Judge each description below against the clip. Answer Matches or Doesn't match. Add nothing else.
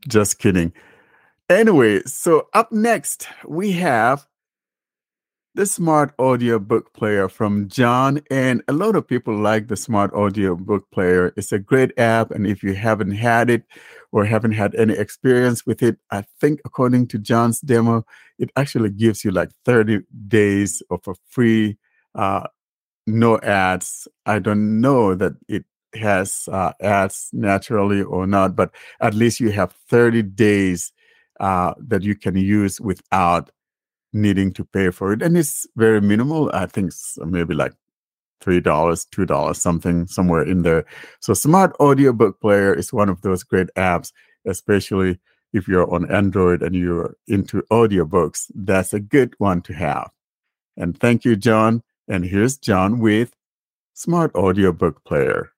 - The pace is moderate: Matches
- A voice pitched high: Doesn't match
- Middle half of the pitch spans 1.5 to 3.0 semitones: Doesn't match